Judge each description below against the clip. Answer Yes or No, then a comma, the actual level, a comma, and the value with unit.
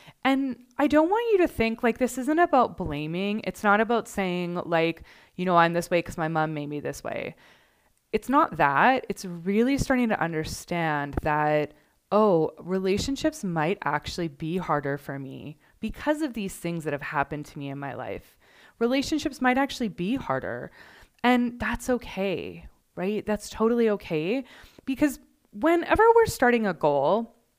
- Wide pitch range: Yes, wide, 8.1 semitones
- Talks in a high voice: Yes, high, 200 Hz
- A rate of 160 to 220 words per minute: Yes, average, 165 wpm